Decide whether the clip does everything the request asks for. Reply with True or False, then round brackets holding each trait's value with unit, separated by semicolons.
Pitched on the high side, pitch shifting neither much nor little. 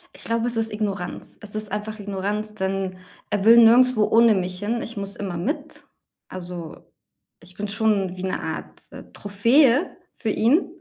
True (210 Hz; 3.0 semitones)